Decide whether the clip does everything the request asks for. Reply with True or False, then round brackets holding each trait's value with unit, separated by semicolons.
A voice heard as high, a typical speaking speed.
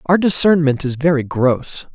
False (150 Hz; 155 wpm)